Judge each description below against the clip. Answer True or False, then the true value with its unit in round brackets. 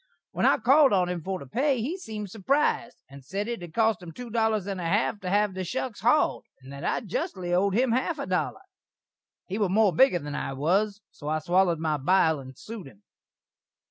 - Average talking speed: False (225 wpm)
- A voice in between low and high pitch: False (195 Hz)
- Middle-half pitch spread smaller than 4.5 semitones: False (5.3 semitones)